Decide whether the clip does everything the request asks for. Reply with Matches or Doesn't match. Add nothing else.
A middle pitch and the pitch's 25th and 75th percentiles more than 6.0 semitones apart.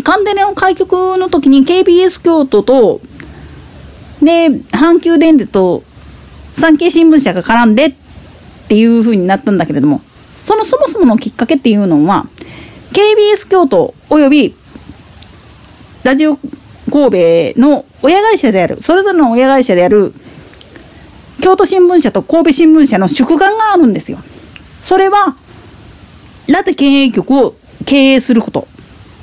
Doesn't match